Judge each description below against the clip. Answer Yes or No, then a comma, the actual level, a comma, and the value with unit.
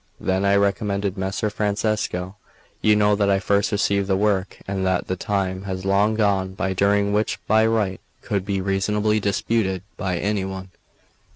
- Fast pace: No, average, 170 wpm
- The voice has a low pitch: Yes, low, 100 Hz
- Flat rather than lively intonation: Yes, narrow, 1.5 semitones